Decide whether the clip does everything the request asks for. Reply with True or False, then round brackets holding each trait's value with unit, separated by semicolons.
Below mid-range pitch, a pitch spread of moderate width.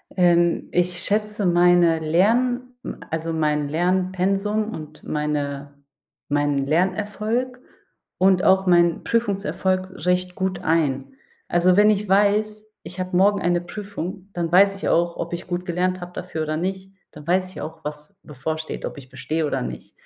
False (180 Hz; 3.5 semitones)